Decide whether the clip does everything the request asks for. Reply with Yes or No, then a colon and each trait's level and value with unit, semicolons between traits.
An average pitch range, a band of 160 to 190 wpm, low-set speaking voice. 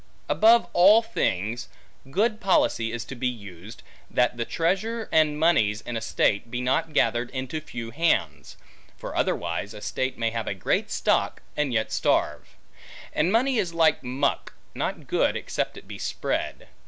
No: wide, 6.8 semitones; average, 165 wpm; low, 130 Hz